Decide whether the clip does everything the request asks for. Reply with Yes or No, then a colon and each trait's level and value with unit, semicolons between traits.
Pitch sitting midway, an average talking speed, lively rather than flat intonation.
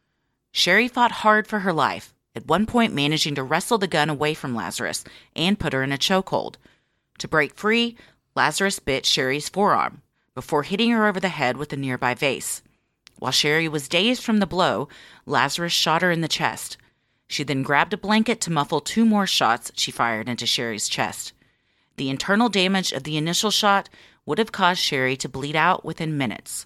Yes: medium, 160 Hz; average, 190 wpm; wide, 6.2 semitones